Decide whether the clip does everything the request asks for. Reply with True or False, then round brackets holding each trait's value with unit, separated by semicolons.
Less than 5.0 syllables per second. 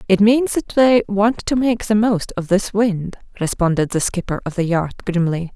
True (4.5 syllables/s)